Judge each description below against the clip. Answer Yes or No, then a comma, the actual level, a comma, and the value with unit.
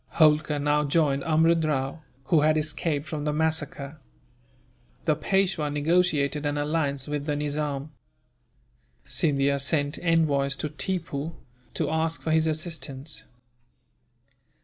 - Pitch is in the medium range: Yes, medium, 150 Hz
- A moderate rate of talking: No, slow, 120 wpm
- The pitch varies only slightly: Yes, narrow, 1.9 semitones